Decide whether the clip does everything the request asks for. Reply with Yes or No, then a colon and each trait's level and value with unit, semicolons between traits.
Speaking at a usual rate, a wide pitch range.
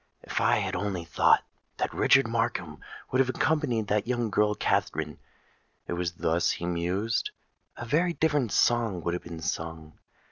Yes: average, 150 wpm; wide, 5.8 semitones